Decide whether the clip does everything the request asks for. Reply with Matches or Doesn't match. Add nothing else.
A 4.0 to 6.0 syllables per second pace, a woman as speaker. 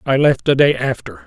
Doesn't match